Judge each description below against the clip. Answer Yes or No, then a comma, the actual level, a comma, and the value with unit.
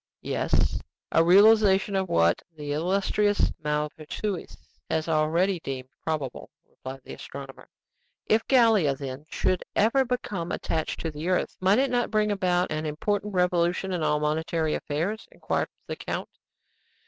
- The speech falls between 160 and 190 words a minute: No, average, 140 wpm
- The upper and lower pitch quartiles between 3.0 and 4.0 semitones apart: No, average, 5.1 semitones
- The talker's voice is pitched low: No, medium, 175 Hz